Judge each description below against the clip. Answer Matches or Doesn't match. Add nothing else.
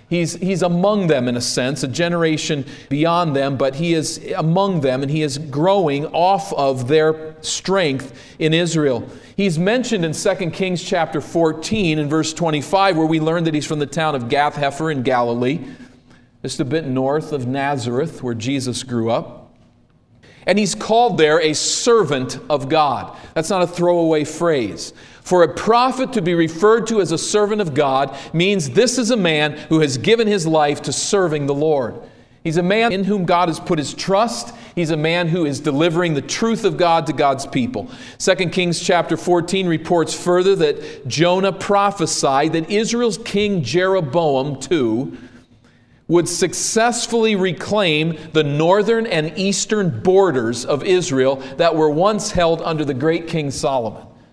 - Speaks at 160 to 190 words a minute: Matches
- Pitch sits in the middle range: Matches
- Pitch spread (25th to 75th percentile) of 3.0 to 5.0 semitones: Matches